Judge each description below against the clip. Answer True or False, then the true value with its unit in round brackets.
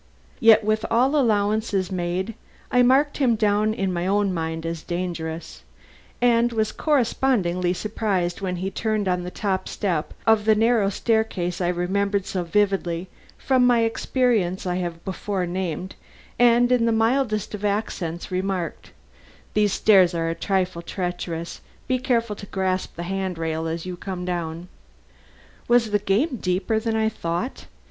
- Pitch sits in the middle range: False (195 Hz)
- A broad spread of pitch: False (3.9 semitones)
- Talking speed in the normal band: True (155 wpm)